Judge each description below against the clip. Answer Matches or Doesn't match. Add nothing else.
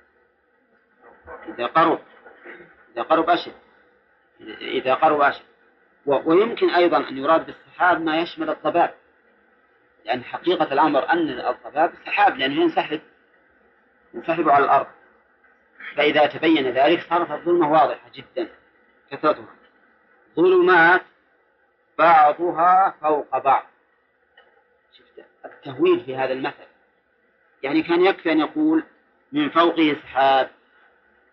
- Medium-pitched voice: Matches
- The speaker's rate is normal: Matches